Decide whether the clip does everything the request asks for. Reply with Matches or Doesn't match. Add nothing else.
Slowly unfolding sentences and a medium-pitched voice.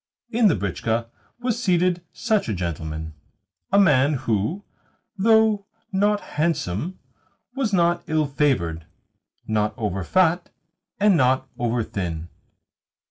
Matches